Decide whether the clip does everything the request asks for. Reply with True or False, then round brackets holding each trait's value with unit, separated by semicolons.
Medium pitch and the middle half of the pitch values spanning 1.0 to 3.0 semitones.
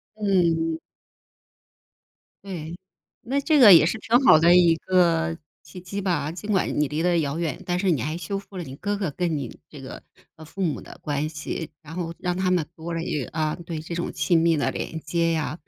True (170 Hz; 2.7 semitones)